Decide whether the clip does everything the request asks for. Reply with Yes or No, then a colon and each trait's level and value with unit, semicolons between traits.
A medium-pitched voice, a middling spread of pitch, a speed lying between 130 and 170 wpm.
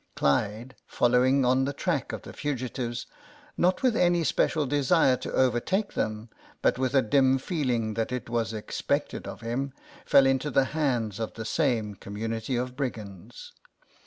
No: low, 125 Hz; average, 3.5 semitones; average, 160 wpm